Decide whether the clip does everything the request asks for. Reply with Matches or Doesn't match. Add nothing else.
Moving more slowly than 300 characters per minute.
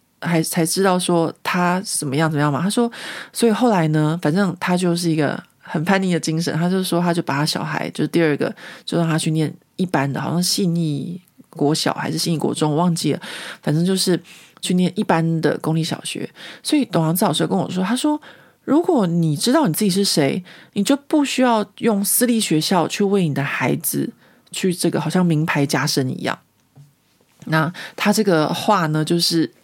Matches